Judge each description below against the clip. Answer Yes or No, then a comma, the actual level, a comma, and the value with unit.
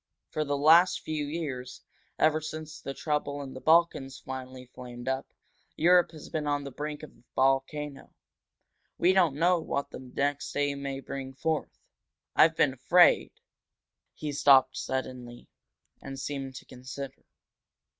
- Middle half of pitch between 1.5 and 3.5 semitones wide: Yes, average, 2.8 semitones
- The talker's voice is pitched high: No, medium, 140 Hz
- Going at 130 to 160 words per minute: Yes, average, 150 wpm